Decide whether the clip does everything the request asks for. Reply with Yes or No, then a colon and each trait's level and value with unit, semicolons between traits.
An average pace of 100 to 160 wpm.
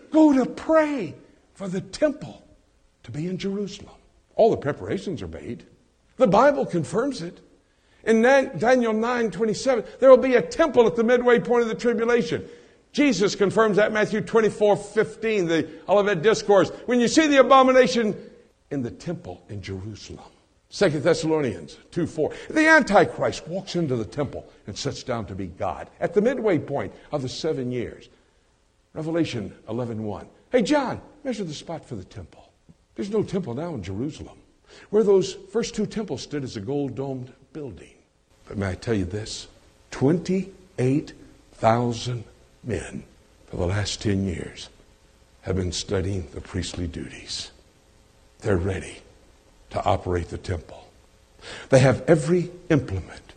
Yes: average, 150 wpm